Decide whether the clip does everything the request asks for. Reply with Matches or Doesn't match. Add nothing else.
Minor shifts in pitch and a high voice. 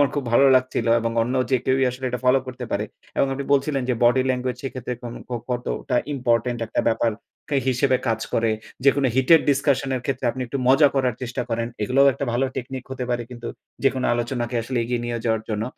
Doesn't match